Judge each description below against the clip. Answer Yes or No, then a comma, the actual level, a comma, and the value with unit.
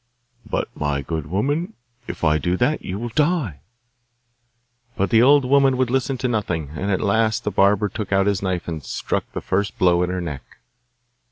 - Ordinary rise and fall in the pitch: No, wide, 6.2 semitones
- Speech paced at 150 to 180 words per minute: No, average, 190 wpm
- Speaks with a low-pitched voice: Yes, low, 100 Hz